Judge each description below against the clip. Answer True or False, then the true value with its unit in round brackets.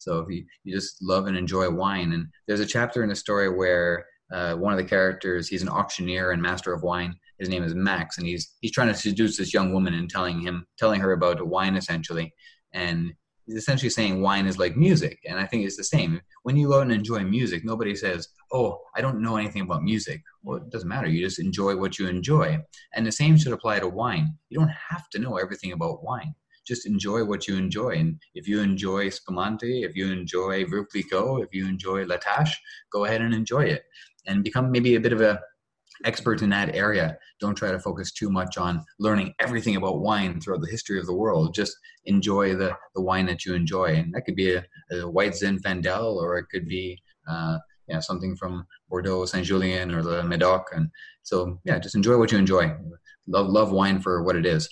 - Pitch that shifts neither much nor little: True (3.6 semitones)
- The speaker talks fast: True (220 wpm)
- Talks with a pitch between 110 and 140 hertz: False (95 Hz)